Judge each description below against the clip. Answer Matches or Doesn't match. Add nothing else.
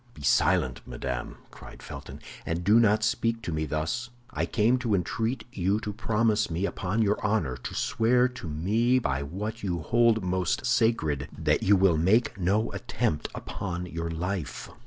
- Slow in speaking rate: Doesn't match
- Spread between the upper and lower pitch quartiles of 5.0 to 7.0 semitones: Matches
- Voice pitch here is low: Matches